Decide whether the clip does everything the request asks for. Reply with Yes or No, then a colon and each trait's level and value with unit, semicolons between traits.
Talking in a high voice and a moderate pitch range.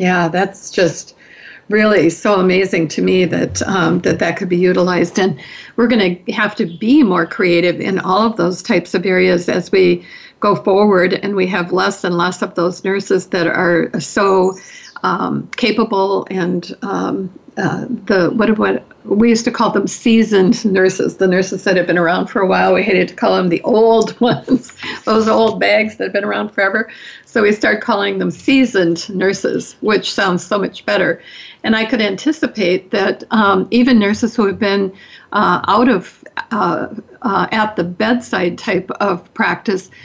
Yes: high, 195 Hz; average, 3.3 semitones